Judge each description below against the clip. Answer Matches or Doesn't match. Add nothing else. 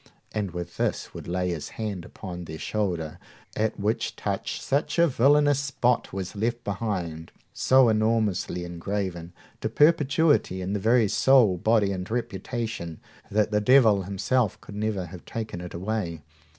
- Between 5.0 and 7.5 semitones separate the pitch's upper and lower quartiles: Doesn't match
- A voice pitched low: Matches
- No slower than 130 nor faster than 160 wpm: Matches